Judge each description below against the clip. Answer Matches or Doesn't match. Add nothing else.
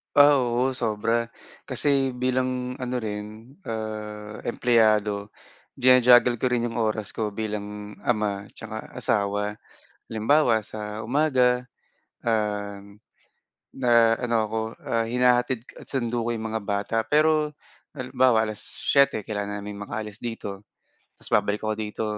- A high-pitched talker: Doesn't match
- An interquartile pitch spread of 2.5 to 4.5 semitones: Matches